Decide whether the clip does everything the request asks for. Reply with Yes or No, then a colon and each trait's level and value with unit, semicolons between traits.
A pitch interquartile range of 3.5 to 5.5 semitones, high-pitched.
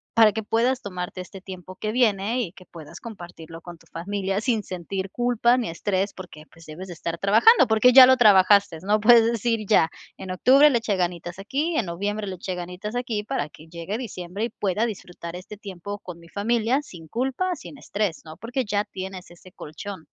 Yes: average, 4.3 semitones; high, 200 Hz